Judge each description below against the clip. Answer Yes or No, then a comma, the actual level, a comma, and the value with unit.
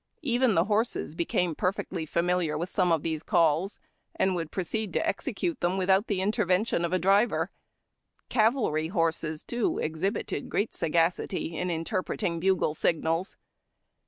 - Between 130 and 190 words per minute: Yes, average, 145 wpm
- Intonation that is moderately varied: Yes, average, 3.4 semitones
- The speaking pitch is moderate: Yes, medium, 180 Hz